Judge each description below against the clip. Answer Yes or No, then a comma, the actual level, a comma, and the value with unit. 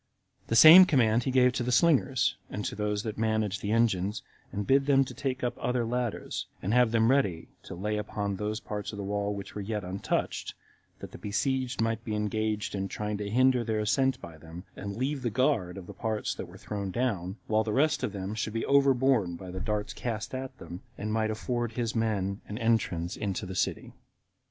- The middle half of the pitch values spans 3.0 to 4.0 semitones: Yes, average, 3.6 semitones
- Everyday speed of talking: No, fast, 215 wpm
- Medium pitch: No, low, 110 Hz